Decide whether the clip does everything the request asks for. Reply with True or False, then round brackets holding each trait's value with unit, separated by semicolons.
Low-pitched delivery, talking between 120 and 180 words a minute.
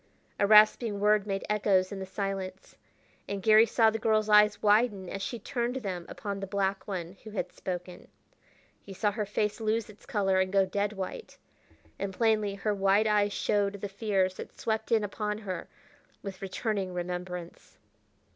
False (200 Hz; 175 wpm)